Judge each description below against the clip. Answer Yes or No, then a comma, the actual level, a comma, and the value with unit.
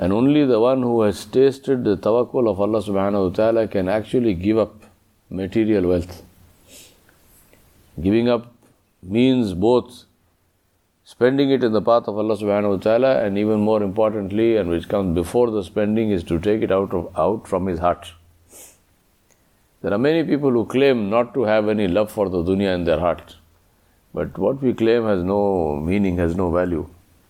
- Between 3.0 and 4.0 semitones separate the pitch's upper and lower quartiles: Yes, average, 3.6 semitones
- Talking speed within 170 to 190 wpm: Yes, average, 180 wpm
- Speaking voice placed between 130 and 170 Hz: No, low, 100 Hz